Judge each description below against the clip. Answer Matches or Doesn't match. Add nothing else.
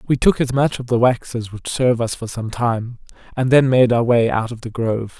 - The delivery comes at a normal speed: Doesn't match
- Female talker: Doesn't match